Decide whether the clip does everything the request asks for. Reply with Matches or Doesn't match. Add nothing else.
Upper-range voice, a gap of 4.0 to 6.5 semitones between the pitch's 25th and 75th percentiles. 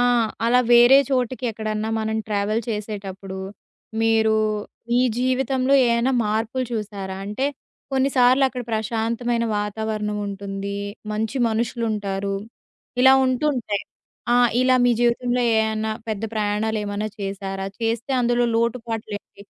Doesn't match